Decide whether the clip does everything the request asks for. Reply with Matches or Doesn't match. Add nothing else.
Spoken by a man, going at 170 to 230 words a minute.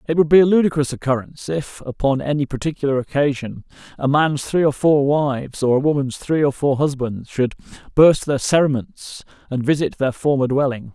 Matches